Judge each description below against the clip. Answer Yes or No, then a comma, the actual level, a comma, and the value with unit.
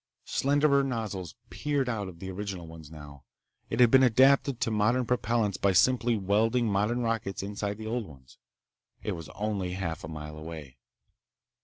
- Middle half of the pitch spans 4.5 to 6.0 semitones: Yes, wide, 5.4 semitones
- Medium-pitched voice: No, low, 105 Hz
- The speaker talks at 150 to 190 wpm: Yes, average, 165 wpm